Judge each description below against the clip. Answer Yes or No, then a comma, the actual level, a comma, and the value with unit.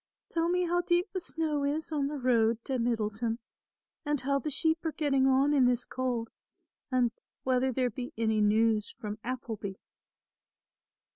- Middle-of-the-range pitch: No, very high, 260 Hz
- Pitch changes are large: No, average, 4.4 semitones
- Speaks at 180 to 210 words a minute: No, average, 160 wpm